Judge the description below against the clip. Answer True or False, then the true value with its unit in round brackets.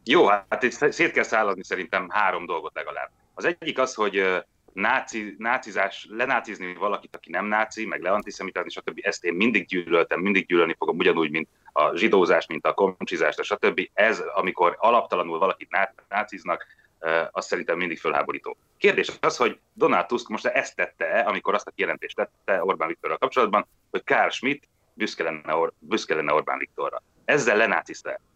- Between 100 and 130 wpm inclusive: False (155 wpm)